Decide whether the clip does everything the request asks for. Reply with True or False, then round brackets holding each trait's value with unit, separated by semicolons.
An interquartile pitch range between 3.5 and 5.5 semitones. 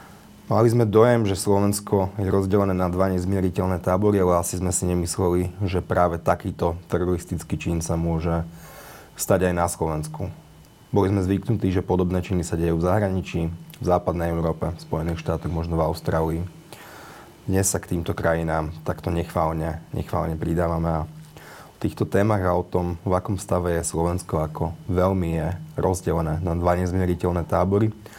False (2.5 semitones)